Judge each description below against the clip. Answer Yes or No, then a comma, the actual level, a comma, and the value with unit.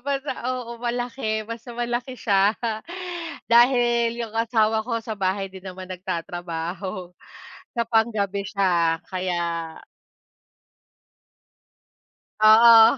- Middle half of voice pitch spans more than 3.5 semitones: Yes, average, 4.1 semitones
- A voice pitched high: Yes, high, 215 Hz